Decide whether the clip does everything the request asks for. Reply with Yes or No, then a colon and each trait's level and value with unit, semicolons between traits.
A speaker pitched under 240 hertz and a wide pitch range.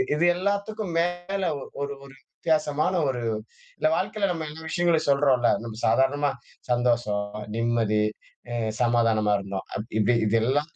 Yes: medium, 140 Hz; wide, 6.6 semitones